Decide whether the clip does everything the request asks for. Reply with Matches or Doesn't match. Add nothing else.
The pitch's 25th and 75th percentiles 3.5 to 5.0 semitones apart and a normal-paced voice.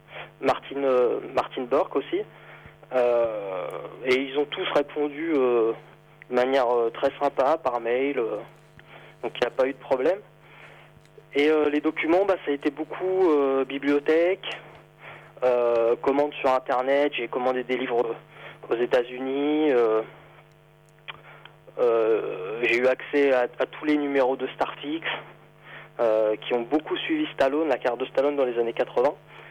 Matches